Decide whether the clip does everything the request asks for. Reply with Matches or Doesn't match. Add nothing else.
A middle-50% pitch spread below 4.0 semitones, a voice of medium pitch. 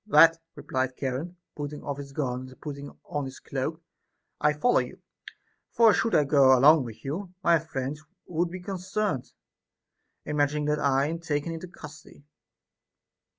Matches